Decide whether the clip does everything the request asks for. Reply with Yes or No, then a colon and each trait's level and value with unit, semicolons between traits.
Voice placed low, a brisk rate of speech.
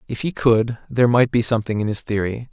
Yes: low, 115 Hz; fast, 240 wpm